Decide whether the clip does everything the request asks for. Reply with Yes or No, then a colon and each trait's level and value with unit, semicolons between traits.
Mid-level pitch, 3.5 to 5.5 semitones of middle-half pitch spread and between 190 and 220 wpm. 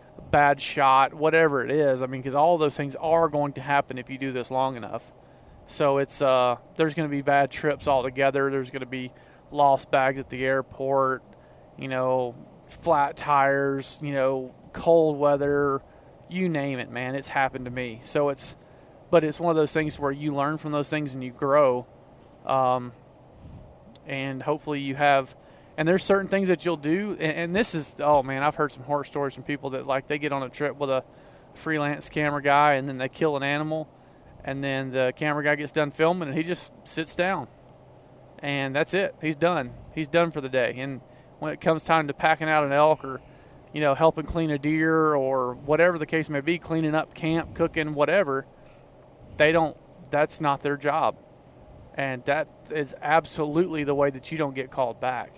No: medium, 145 Hz; average, 2.8 semitones; average, 200 wpm